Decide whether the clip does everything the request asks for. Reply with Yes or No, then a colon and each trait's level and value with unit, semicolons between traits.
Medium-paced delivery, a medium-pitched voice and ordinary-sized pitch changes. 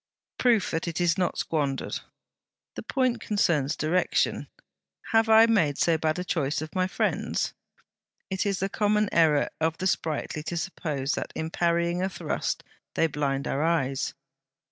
Yes: average, 160 wpm; medium, 170 Hz; average, 3.8 semitones